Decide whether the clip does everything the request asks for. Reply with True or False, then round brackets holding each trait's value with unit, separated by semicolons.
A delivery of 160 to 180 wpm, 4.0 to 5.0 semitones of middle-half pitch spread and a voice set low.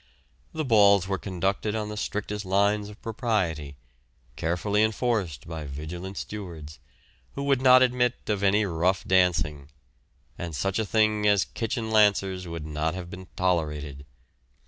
False (145 wpm; 4.3 semitones; 95 Hz)